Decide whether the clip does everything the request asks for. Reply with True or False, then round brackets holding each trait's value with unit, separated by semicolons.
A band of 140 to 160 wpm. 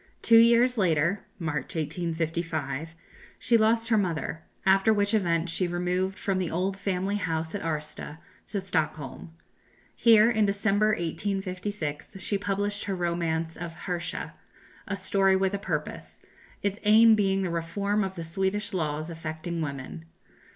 True (145 wpm)